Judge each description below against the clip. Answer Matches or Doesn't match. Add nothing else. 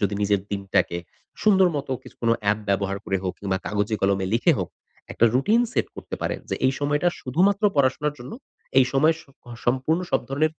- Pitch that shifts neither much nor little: Doesn't match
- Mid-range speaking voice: Doesn't match